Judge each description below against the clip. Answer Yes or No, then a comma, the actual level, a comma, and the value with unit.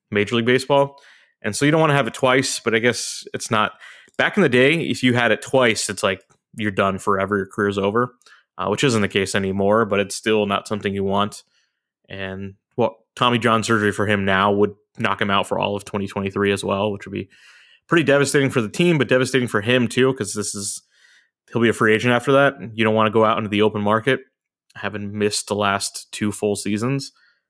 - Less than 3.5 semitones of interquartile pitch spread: No, average, 3.8 semitones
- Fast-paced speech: Yes, fast, 230 wpm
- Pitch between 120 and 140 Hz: No, low, 110 Hz